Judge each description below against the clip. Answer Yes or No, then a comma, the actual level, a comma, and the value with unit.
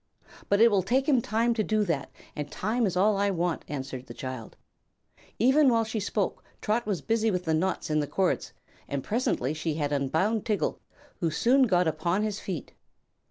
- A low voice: No, high, 195 Hz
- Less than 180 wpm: No, average, 195 wpm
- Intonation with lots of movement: Yes, wide, 6.0 semitones